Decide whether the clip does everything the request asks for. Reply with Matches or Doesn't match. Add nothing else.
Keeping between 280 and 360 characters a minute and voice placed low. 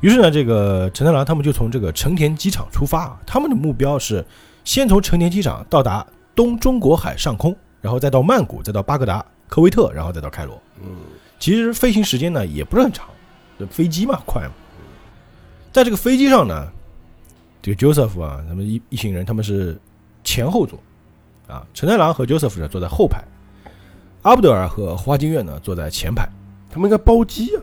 Matches